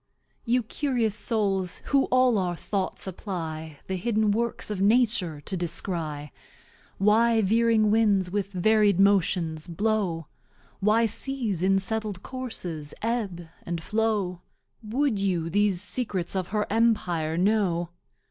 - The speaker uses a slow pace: Yes, slow, 125 wpm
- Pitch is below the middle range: No, high, 200 Hz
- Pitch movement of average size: Yes, average, 4.0 semitones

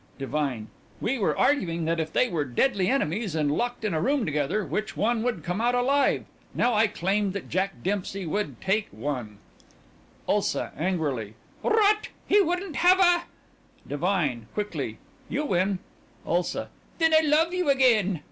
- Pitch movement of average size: No, wide, 8.7 semitones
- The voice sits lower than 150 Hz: No, high, 200 Hz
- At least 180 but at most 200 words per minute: No, average, 155 wpm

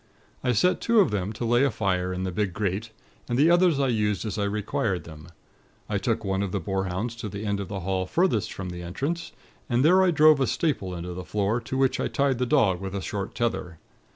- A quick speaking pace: Yes, fast, 240 wpm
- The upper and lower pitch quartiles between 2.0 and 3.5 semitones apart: No, average, 5.1 semitones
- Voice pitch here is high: No, low, 105 Hz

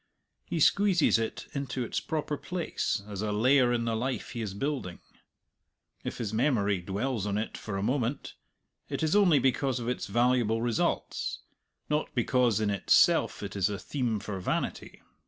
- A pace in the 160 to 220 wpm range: Yes, average, 170 wpm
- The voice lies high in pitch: No, low, 120 Hz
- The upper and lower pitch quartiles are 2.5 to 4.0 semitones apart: No, average, 4.7 semitones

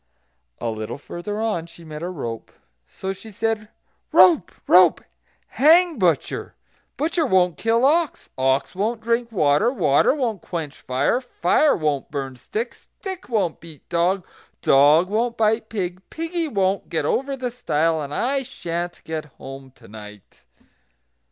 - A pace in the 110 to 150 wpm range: Yes, average, 145 wpm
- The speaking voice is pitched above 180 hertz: Yes, high, 190 Hz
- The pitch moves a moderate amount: No, wide, 7.7 semitones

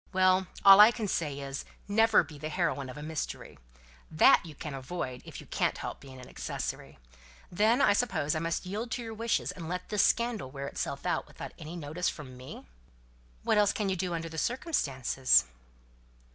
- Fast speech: No, average, 195 wpm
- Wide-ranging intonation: Yes, wide, 6.4 semitones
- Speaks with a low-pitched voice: No, medium, 170 Hz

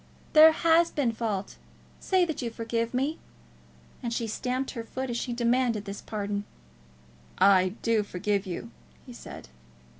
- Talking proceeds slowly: No, average, 150 wpm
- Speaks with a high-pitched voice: Yes, high, 230 Hz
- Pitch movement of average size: Yes, average, 4.0 semitones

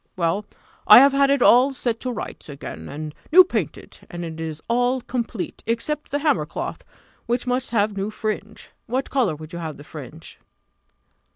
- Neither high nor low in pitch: No, high, 220 Hz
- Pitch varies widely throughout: Yes, wide, 7.6 semitones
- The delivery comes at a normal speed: Yes, average, 180 wpm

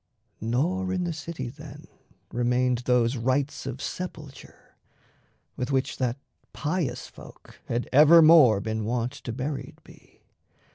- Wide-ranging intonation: No, average, 4.2 semitones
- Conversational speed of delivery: No, slow, 125 wpm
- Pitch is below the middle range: Yes, low, 130 Hz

